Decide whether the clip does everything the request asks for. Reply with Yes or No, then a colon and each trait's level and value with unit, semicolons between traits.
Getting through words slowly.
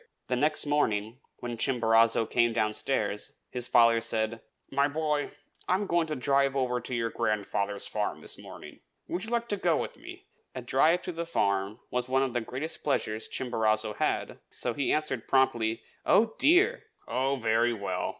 No: average, 175 wpm